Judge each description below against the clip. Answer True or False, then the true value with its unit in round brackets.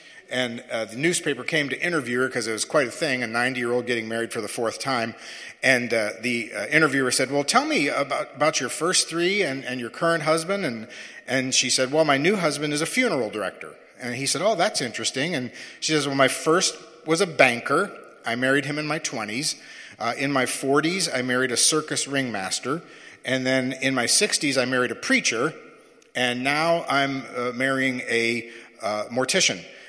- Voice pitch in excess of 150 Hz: False (135 Hz)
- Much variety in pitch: False (3.9 semitones)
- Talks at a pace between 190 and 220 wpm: True (205 wpm)